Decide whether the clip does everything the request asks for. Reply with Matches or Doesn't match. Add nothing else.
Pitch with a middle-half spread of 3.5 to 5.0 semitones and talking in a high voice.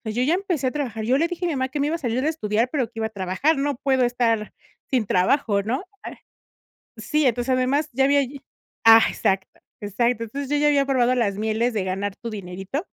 Matches